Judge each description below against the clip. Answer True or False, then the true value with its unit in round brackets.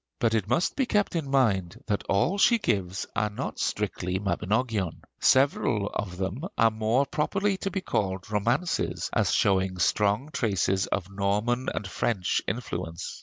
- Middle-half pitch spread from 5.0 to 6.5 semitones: True (5.3 semitones)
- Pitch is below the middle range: True (105 Hz)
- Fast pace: False (155 wpm)